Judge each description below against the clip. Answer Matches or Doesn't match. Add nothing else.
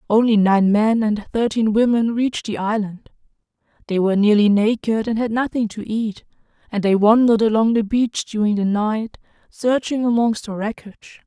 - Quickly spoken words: Doesn't match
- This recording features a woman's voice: Matches